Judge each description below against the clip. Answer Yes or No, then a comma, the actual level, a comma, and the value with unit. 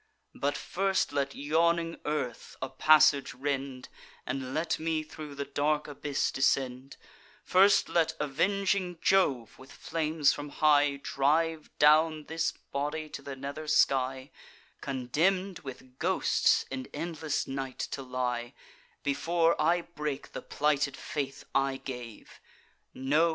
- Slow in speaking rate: Yes, slow, 125 wpm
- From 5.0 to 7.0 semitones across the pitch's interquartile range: No, average, 3.1 semitones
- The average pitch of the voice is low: No, medium, 145 Hz